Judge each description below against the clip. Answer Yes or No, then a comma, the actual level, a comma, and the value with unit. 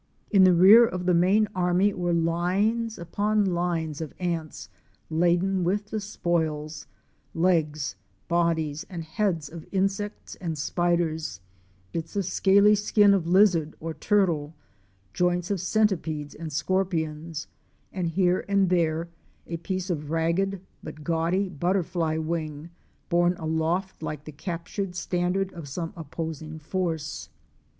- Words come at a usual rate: No, slow, 130 wpm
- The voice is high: No, medium, 175 Hz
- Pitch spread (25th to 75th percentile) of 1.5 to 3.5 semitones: Yes, average, 3.0 semitones